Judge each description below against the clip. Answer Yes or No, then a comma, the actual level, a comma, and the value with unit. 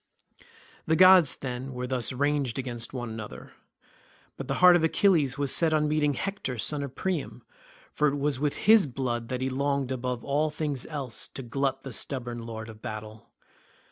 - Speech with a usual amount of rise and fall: Yes, average, 3.4 semitones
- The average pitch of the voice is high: No, low, 135 Hz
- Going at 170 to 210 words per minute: Yes, average, 180 wpm